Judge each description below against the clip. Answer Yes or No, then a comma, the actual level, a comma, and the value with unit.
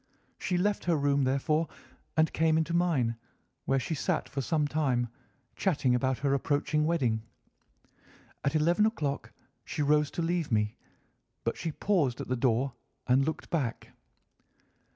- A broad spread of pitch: No, average, 3.7 semitones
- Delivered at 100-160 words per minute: Yes, average, 150 wpm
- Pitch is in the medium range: Yes, medium, 145 Hz